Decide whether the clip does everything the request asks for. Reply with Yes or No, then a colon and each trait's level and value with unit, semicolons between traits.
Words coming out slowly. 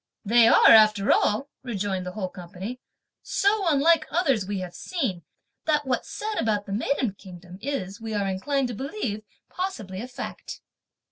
No: average, 160 wpm